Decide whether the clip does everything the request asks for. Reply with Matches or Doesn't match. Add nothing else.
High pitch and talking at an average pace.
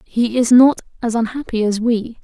Matches